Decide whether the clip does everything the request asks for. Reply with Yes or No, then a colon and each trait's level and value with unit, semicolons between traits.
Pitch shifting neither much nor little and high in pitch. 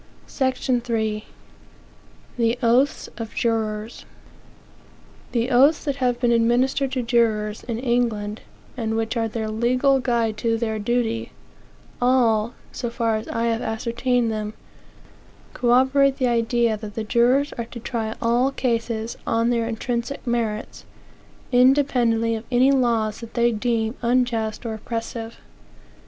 No: narrow, 1.8 semitones; high, 235 Hz